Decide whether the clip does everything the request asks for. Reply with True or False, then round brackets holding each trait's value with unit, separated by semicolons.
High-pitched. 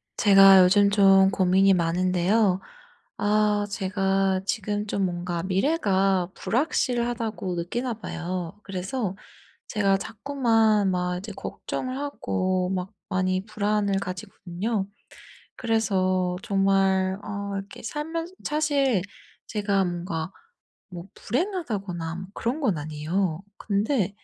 True (195 Hz)